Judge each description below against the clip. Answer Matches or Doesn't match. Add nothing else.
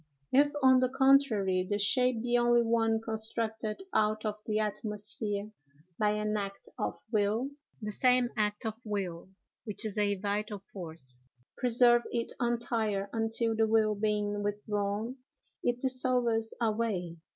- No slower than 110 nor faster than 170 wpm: Matches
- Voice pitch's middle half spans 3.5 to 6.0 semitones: Doesn't match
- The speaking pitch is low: Doesn't match